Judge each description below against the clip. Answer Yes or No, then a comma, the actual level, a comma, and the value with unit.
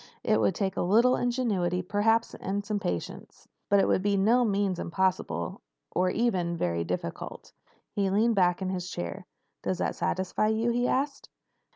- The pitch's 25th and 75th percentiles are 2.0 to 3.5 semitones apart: No, average, 4.0 semitones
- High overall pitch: Yes, high, 195 Hz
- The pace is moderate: Yes, average, 170 wpm